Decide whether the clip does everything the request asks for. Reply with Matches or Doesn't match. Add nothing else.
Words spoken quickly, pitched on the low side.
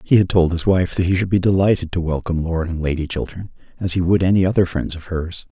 Matches